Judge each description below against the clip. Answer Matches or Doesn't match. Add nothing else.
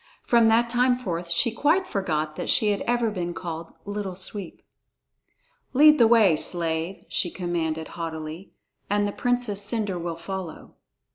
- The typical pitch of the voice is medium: Doesn't match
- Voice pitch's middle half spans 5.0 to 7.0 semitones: Matches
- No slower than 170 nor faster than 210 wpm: Doesn't match